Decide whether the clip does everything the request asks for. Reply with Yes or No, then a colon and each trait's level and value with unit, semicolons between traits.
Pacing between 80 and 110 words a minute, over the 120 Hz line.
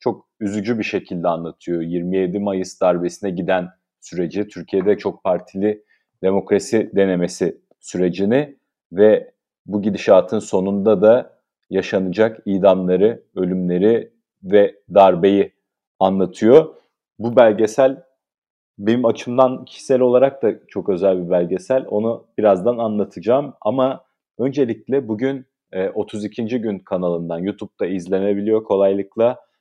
No: average, 100 wpm; low, 105 Hz